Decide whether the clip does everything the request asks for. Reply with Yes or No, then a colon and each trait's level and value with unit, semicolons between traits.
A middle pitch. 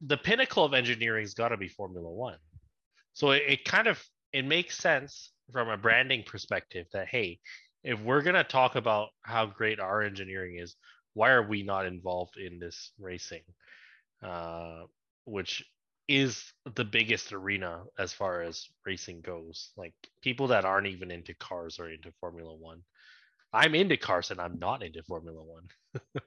No: low, 100 Hz